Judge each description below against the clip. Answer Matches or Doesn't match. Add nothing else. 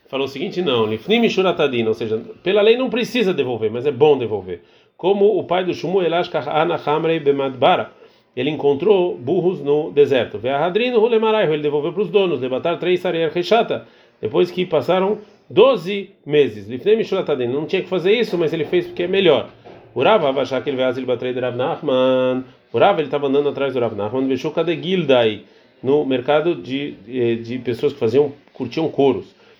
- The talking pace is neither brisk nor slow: Matches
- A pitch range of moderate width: Doesn't match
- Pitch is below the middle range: Doesn't match